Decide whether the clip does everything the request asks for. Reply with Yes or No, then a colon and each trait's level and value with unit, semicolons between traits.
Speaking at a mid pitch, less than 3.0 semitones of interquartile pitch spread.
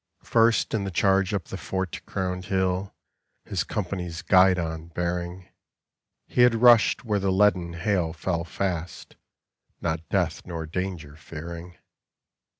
No: very low, 90 Hz; narrow, 2.4 semitones